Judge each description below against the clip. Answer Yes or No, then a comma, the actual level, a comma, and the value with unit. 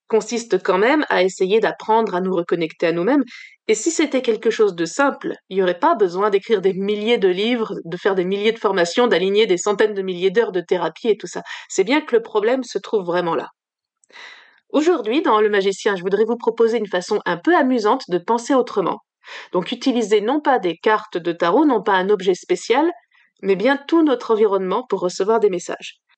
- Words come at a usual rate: Yes, average, 210 wpm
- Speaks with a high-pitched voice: Yes, high, 225 Hz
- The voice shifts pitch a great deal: Yes, wide, 7.0 semitones